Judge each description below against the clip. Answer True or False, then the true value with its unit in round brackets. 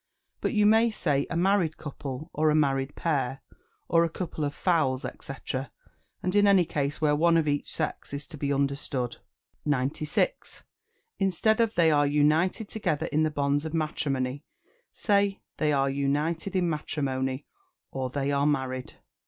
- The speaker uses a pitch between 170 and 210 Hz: False (150 Hz)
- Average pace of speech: True (160 wpm)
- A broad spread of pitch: False (3.5 semitones)